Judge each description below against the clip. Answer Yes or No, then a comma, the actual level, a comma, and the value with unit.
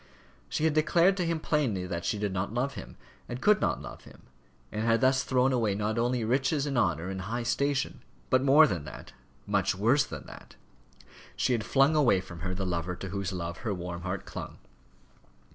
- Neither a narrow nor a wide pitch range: No, wide, 6.5 semitones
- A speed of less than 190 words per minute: No, fast, 205 wpm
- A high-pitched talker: No, low, 115 Hz